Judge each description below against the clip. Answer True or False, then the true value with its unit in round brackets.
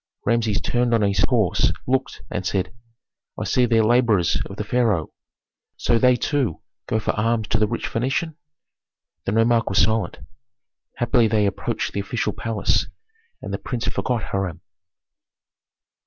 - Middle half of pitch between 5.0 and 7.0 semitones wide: False (3.0 semitones)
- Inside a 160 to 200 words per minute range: False (150 wpm)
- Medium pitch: False (115 Hz)